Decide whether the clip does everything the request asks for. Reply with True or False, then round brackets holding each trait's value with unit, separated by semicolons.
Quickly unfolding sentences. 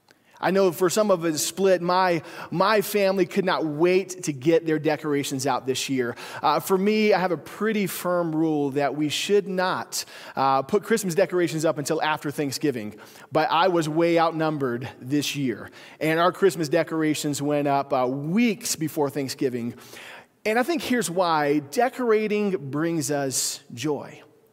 False (165 wpm)